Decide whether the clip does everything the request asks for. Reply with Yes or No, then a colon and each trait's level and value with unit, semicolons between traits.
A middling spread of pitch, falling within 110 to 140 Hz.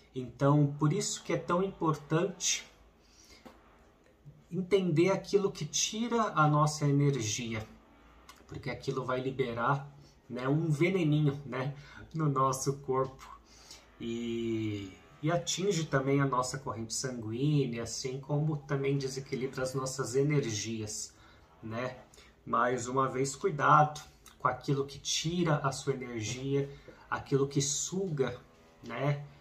Yes: average, 3.5 semitones; low, 135 Hz